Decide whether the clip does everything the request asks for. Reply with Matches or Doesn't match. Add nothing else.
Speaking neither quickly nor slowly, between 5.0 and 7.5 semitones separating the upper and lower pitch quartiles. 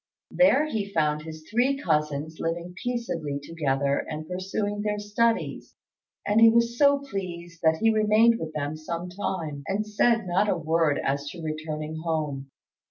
Matches